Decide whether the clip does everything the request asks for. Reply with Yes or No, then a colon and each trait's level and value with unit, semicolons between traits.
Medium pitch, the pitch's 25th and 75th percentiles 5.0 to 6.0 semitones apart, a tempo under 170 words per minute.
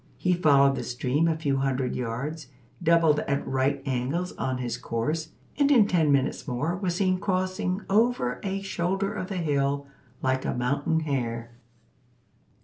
Yes: medium, 150 Hz; wide, 5.5 semitones; average, 155 wpm